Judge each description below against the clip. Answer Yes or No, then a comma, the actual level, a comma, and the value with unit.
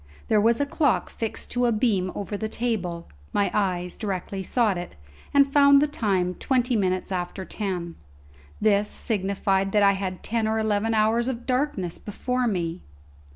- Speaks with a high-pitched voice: Yes, high, 210 Hz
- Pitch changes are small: No, average, 4.0 semitones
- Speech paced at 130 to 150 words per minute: No, average, 165 wpm